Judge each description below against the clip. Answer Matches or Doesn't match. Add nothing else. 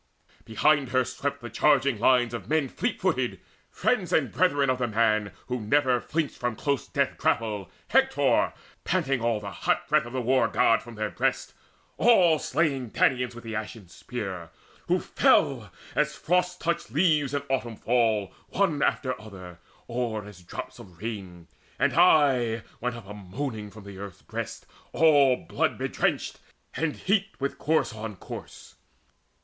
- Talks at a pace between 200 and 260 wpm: Doesn't match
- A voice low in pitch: Matches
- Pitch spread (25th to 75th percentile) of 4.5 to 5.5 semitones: Matches